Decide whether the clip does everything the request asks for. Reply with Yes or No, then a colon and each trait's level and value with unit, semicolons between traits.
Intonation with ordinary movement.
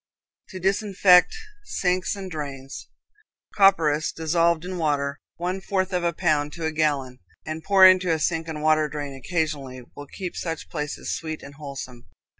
Yes: average, 3.6 semitones